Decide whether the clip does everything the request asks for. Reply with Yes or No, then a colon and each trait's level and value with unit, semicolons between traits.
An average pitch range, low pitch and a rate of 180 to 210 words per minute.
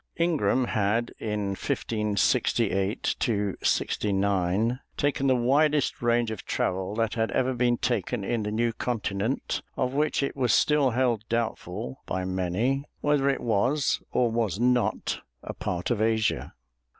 No: average, 3.7 semitones; low, 115 Hz; average, 140 wpm